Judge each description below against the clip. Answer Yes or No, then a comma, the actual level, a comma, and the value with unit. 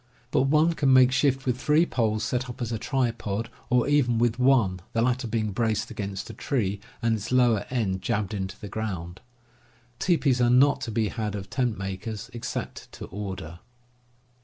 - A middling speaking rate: Yes, average, 185 wpm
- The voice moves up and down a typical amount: Yes, average, 3.7 semitones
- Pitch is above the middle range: No, low, 115 Hz